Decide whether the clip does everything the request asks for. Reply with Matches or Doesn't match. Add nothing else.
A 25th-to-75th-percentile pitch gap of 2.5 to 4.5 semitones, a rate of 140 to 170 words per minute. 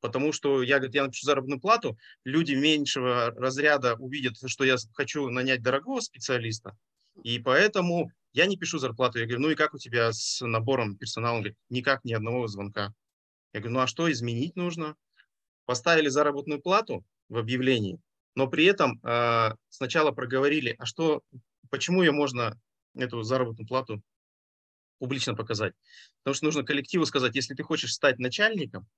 Matches